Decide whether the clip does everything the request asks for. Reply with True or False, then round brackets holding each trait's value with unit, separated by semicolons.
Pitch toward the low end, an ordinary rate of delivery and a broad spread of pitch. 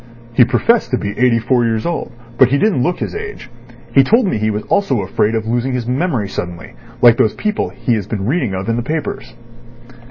False (120 Hz; 220 wpm; 5.8 semitones)